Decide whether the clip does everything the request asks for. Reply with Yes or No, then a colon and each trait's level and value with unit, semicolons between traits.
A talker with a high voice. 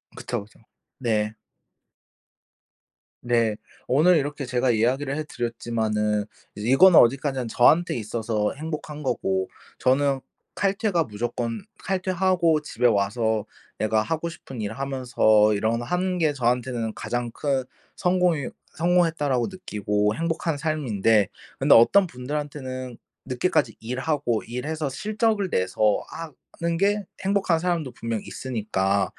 No: low, 130 Hz